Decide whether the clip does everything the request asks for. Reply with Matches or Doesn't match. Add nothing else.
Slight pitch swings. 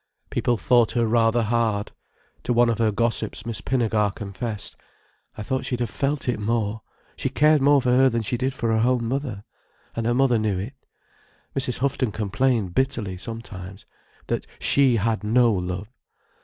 Doesn't match